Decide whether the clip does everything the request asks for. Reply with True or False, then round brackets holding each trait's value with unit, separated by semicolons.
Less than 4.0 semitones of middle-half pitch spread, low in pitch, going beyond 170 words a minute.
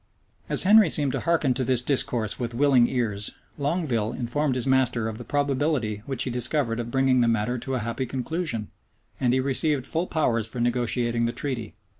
True (3.2 semitones; 125 Hz; 190 wpm)